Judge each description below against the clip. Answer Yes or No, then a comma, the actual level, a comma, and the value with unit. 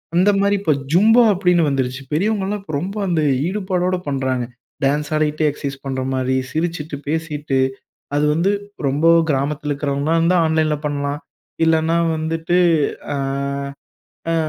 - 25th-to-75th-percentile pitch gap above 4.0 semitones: No, average, 3.6 semitones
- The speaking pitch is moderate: Yes, medium, 155 Hz